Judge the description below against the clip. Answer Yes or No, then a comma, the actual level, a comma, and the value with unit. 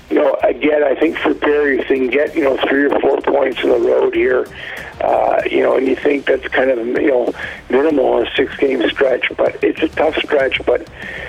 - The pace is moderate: No, fast, 235 wpm